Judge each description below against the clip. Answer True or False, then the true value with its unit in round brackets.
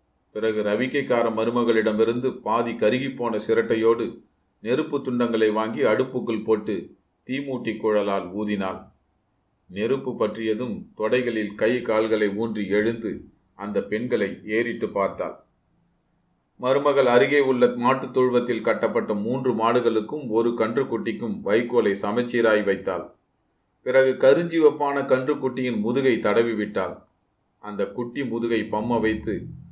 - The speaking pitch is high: False (115 Hz)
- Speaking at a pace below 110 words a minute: True (100 wpm)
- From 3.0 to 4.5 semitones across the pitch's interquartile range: False (2.6 semitones)